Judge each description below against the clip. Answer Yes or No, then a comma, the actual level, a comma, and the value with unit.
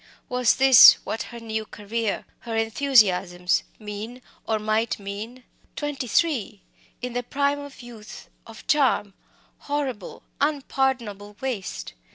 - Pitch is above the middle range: Yes, high, 230 Hz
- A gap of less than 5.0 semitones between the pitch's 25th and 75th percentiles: Yes, average, 4.1 semitones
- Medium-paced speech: No, slow, 120 wpm